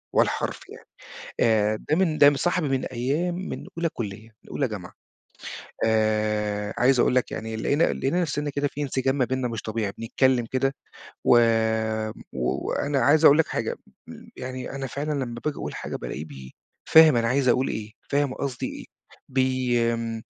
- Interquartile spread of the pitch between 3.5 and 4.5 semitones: Yes, average, 4.2 semitones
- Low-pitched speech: Yes, low, 130 Hz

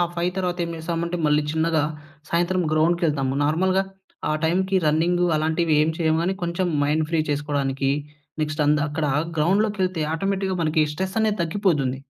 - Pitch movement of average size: Yes, average, 3.2 semitones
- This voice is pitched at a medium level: Yes, medium, 165 Hz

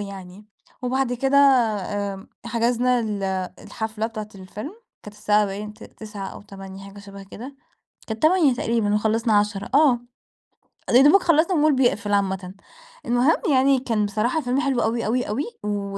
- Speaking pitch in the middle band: No, high, 220 Hz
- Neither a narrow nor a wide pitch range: Yes, average, 4.0 semitones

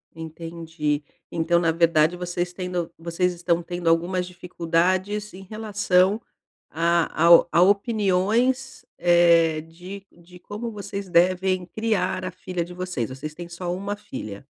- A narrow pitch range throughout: Yes, narrow, 2.1 semitones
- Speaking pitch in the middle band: Yes, medium, 180 Hz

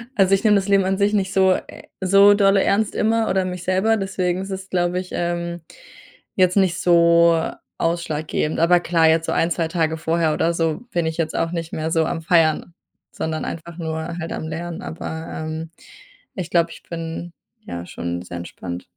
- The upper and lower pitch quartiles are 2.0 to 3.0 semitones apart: Yes, average, 2.7 semitones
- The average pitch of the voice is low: No, medium, 170 Hz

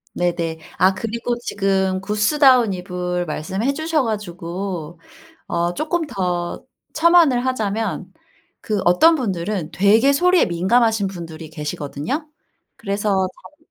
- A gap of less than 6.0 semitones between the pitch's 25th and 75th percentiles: Yes, wide, 5.6 semitones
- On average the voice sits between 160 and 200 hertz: Yes, high, 195 Hz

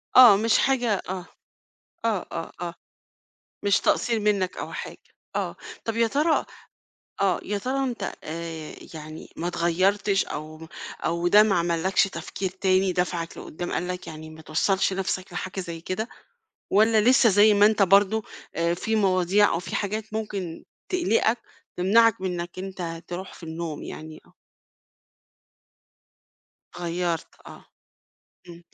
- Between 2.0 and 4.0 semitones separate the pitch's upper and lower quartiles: Yes, average, 3.7 semitones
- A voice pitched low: No, medium, 185 Hz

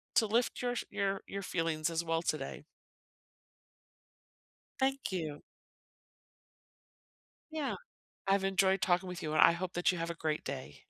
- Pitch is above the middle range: No, medium, 180 Hz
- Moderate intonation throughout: Yes, average, 3.3 semitones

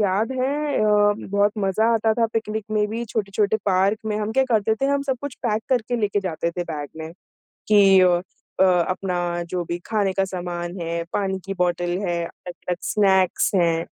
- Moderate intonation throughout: Yes, average, 3.6 semitones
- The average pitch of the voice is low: No, high, 195 Hz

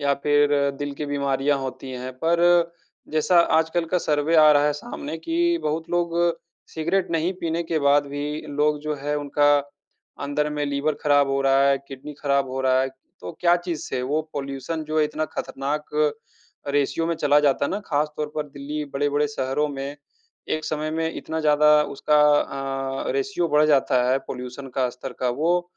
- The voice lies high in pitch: No, medium, 150 Hz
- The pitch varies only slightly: Yes, narrow, 2.3 semitones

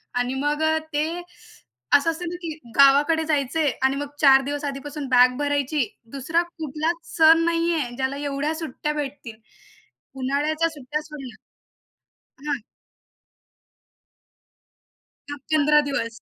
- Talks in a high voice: Yes, very high, 290 Hz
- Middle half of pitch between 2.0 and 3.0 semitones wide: Yes, average, 2.7 semitones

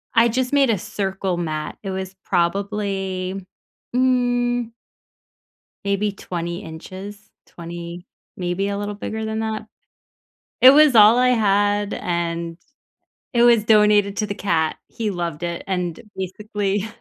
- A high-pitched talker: Yes, high, 200 Hz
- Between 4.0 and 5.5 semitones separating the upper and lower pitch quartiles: No, average, 3.5 semitones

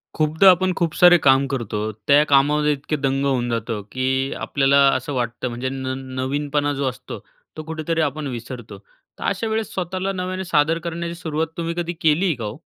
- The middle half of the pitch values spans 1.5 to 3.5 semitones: No, average, 4.4 semitones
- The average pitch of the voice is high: No, medium, 145 Hz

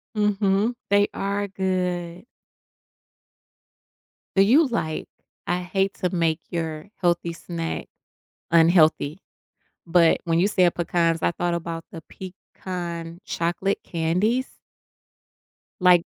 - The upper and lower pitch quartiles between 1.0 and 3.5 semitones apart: Yes, narrow, 2.6 semitones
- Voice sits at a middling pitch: Yes, medium, 175 Hz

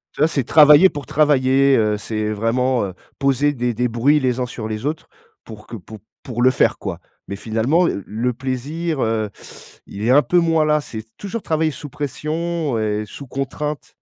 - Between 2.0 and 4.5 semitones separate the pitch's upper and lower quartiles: No, average, 4.9 semitones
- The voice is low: Yes, low, 130 Hz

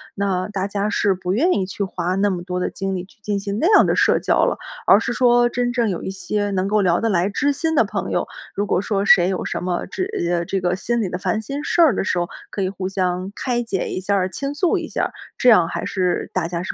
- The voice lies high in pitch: Yes, high, 195 Hz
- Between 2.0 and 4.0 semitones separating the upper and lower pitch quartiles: Yes, average, 3.5 semitones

